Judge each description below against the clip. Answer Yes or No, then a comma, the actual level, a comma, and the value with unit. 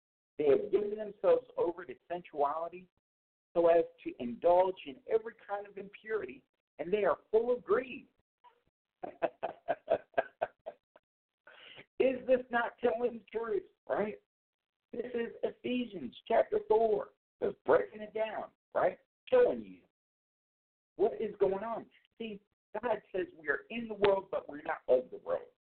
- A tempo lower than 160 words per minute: Yes, average, 140 wpm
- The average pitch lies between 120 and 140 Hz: No, high, 235 Hz